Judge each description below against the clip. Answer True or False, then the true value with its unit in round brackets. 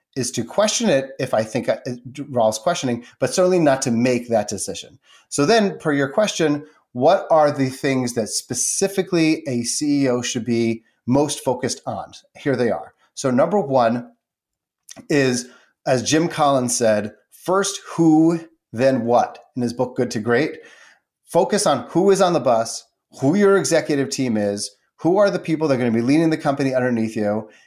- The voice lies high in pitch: False (135 Hz)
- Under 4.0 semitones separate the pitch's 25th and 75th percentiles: False (5.3 semitones)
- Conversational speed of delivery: True (175 wpm)